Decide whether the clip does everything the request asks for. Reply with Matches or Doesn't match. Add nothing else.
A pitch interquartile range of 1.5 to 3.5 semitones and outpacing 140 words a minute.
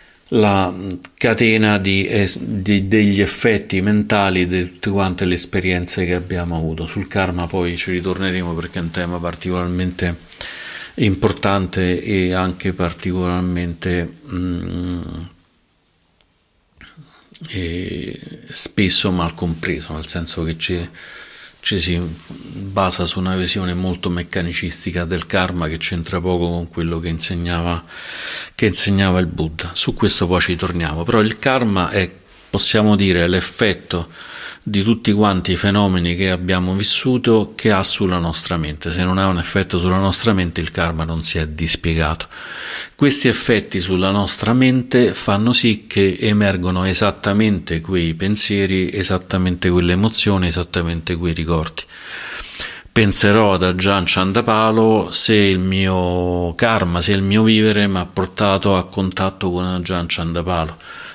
Doesn't match